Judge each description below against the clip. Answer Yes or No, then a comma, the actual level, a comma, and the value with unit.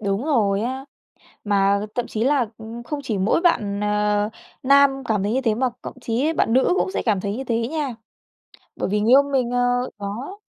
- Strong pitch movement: No, average, 4.3 semitones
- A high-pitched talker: Yes, high, 235 Hz